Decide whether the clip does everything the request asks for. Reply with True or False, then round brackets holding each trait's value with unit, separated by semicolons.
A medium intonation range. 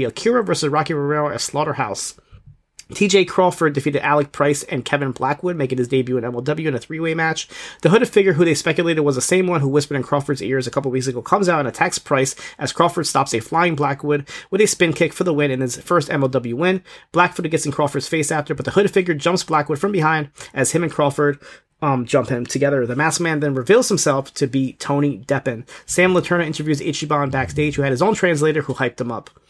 True (3.6 semitones)